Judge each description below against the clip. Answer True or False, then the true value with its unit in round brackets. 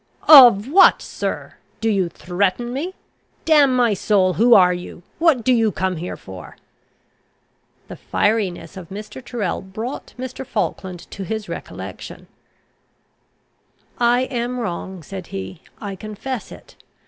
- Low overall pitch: False (215 Hz)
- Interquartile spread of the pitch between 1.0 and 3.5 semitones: False (4.8 semitones)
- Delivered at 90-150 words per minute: True (135 wpm)